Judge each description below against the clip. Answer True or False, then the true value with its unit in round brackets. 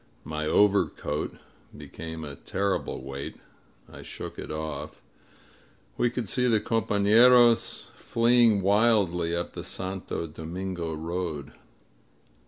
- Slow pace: True (105 wpm)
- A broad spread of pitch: True (5.7 semitones)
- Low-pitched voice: True (95 Hz)